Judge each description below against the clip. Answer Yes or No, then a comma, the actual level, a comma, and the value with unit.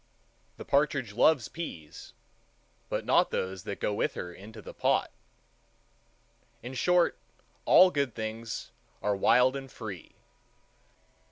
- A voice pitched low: Yes, low, 115 Hz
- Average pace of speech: No, slow, 120 wpm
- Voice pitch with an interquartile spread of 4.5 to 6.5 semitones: Yes, wide, 5.4 semitones